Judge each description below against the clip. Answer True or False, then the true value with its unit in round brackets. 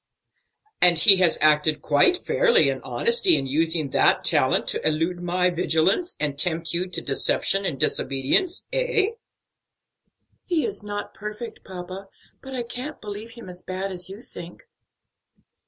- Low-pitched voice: False (185 Hz)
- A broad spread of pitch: True (6.4 semitones)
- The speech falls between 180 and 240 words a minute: False (150 wpm)